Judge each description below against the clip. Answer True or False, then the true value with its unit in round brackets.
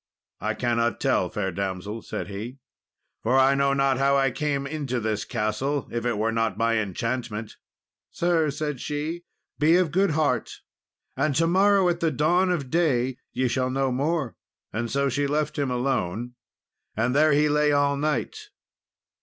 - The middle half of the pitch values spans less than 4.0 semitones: False (4.4 semitones)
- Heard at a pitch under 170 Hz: True (135 Hz)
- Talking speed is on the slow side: False (170 wpm)